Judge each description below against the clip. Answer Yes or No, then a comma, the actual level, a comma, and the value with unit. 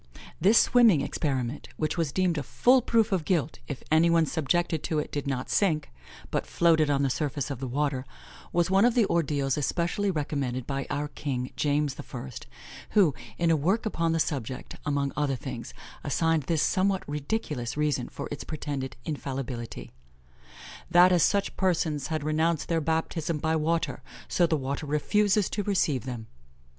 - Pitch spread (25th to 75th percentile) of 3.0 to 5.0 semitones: Yes, average, 3.6 semitones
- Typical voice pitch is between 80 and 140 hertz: No, medium, 155 Hz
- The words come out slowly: No, average, 170 wpm